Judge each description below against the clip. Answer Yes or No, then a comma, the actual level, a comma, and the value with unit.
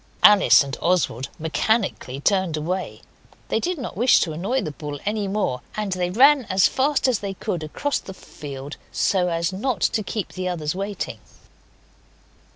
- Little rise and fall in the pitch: No, average, 5.0 semitones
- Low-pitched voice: No, medium, 185 Hz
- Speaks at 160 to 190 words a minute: Yes, average, 165 wpm